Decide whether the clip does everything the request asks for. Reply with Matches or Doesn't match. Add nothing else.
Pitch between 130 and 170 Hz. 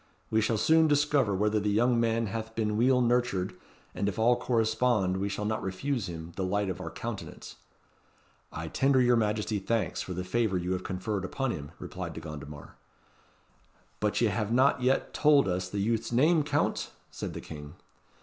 Doesn't match